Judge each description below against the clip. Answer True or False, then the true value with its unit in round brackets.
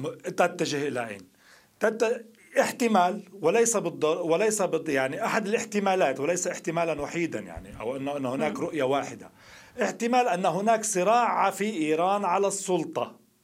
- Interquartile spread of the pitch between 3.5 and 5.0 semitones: False (5.5 semitones)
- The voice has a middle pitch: True (180 Hz)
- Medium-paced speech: True (125 wpm)